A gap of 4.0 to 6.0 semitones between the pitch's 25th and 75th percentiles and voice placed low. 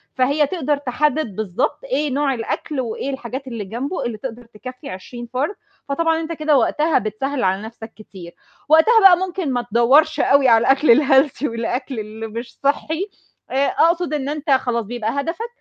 No: average, 4.6 semitones; very high, 270 Hz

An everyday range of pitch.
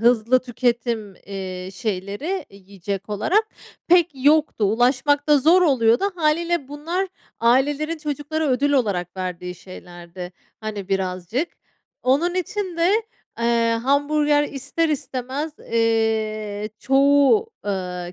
No: wide, 6.9 semitones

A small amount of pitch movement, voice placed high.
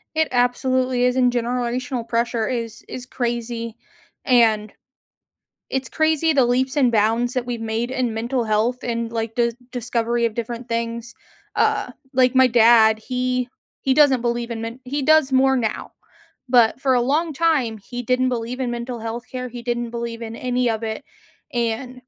Yes: narrow, 1.6 semitones; high, 240 Hz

